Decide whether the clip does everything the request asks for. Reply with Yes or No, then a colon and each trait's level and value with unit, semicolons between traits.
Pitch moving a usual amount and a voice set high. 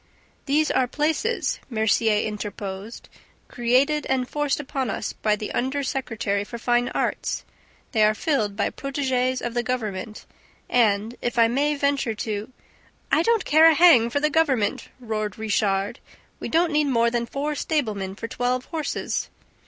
Yes: average, 4.8 semitones; high, 245 Hz